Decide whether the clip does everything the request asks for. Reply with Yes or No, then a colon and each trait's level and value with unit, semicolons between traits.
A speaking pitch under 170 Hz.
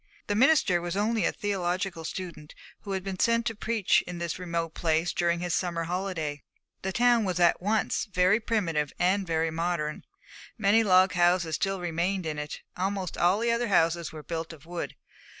No: medium, 180 Hz